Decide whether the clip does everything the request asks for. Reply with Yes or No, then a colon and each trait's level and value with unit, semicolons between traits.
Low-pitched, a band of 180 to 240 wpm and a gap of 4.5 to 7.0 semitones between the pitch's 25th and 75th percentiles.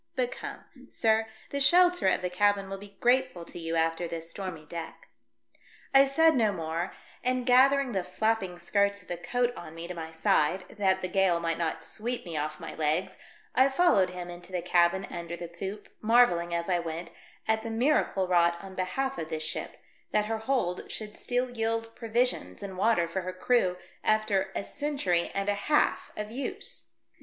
No: high, 195 Hz; average, 190 wpm; average, 5.1 semitones